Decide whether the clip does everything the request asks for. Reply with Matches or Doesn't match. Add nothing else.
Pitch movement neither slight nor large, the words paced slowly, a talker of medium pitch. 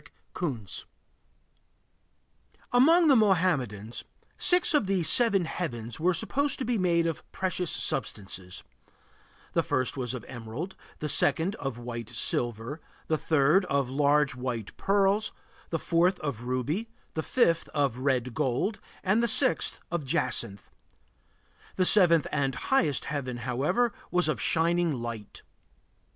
Doesn't match